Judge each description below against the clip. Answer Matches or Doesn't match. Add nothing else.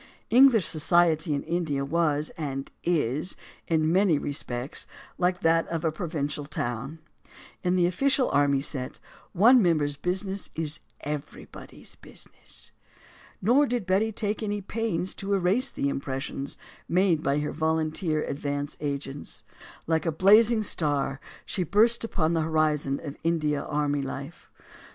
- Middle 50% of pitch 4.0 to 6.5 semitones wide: Matches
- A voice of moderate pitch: Matches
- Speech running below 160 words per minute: Matches